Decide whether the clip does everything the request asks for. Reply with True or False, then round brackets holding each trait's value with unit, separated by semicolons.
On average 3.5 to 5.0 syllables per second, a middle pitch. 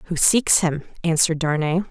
False (5.6 syllables/s; 165 Hz)